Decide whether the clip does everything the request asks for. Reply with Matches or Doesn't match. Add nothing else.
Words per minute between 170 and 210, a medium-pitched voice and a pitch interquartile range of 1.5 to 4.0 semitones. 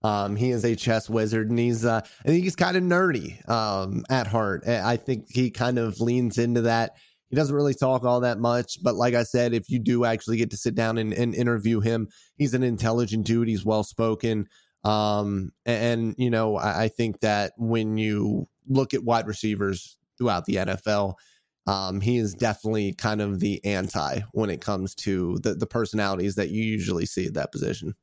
Doesn't match